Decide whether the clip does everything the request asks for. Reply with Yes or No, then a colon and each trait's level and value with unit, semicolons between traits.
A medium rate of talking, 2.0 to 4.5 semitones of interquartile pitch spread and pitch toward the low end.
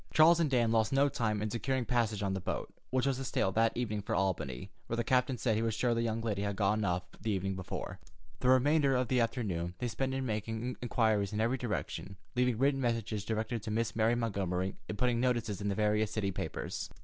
No: fast, 230 wpm; average, 3.3 semitones; low, 115 Hz